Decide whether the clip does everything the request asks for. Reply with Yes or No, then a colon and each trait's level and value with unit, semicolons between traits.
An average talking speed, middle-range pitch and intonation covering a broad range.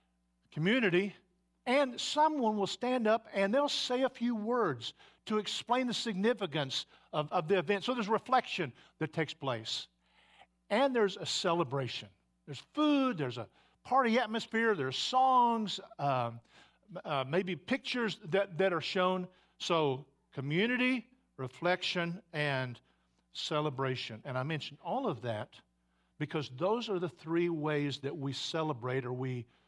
Yes: average, 150 wpm; medium, 180 Hz; wide, 8.7 semitones